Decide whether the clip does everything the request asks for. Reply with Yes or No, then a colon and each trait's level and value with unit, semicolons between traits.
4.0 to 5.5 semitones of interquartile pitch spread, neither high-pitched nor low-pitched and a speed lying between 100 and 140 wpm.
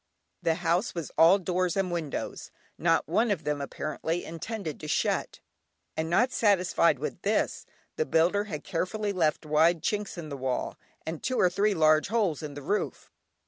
No: average, 4.3 semitones; medium, 170 Hz; average, 175 wpm